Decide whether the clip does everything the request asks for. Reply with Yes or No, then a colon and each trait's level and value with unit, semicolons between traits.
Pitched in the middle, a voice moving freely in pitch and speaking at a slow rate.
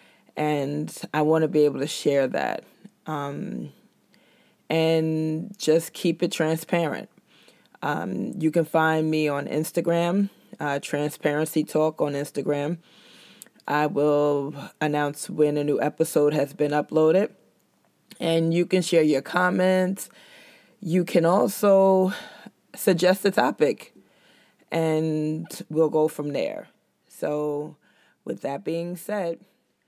No: medium, 160 Hz; average, 2.9 semitones; slow, 120 wpm